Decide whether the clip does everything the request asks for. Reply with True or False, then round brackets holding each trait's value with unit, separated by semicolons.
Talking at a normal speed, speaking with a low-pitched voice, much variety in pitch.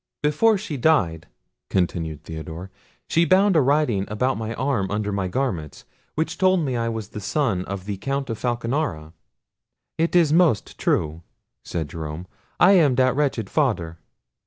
True (155 wpm; 115 Hz; 8.4 semitones)